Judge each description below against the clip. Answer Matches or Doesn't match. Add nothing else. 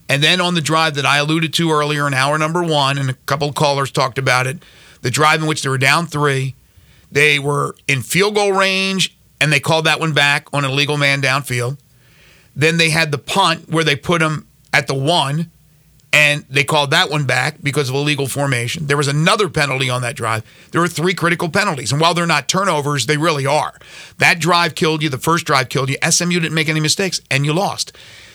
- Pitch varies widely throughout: Doesn't match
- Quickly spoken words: Matches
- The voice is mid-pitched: Matches